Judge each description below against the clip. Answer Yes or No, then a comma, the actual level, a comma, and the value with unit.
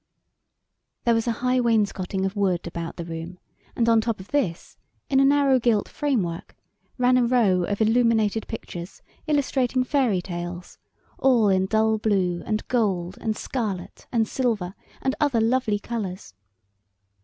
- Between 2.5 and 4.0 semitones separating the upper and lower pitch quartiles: No, average, 4.8 semitones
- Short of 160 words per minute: Yes, average, 150 wpm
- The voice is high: Yes, high, 220 Hz